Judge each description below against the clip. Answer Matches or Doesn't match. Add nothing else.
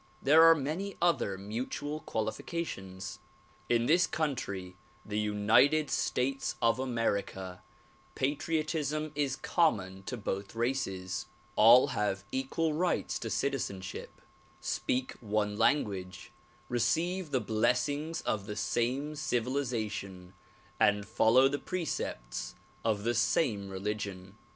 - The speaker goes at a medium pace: Doesn't match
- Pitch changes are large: Matches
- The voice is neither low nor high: Doesn't match